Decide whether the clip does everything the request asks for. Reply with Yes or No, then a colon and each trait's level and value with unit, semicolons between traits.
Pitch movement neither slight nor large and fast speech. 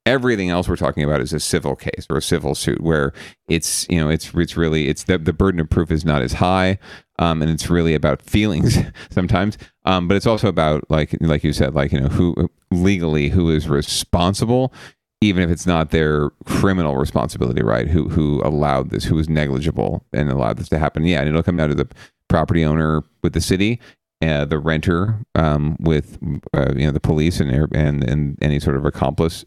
Yes: average, 3.4 semitones; fast, 210 wpm